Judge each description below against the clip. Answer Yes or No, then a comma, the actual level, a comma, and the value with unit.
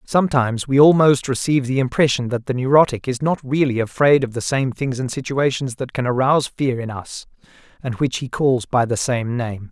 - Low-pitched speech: Yes, low, 130 Hz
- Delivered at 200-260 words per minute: Yes, fast, 205 wpm